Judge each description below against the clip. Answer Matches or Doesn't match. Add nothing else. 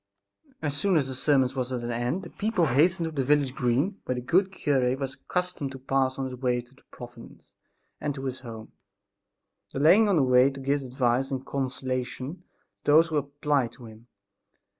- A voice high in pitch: Doesn't match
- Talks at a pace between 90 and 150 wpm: Doesn't match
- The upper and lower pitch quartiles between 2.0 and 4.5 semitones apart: Matches